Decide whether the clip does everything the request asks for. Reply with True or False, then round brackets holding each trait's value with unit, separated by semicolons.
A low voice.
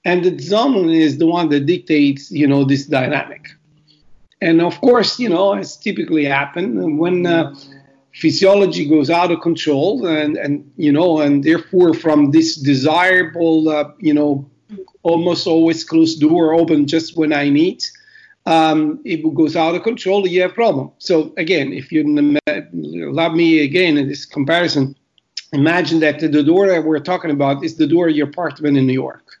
False (160 Hz)